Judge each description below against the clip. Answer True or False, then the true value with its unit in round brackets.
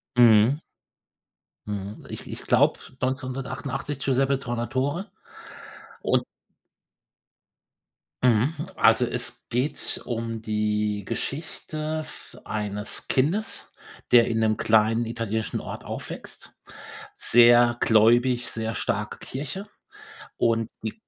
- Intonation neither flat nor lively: True (3.2 semitones)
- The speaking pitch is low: True (120 Hz)